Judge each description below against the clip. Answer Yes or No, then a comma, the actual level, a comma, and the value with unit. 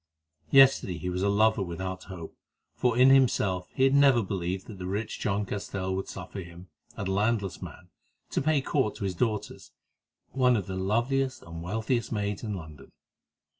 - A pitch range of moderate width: Yes, average, 4.1 semitones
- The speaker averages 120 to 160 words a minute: No, average, 175 wpm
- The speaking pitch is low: Yes, low, 100 Hz